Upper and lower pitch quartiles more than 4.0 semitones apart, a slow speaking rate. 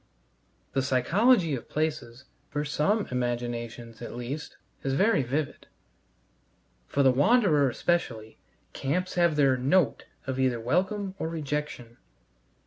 Yes: average, 5.3 semitones; slow, 120 wpm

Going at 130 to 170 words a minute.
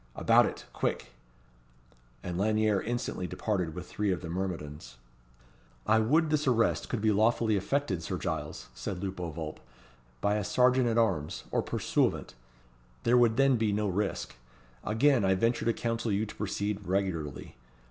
Yes: average, 155 wpm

